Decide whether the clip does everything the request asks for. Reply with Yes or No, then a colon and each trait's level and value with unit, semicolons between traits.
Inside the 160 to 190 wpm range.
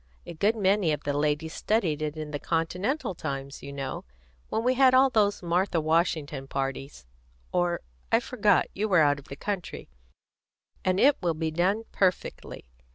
Yes: average, 170 wpm